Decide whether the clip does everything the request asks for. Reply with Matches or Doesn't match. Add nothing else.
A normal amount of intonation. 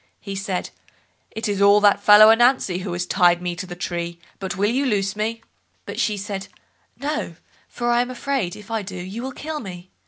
Matches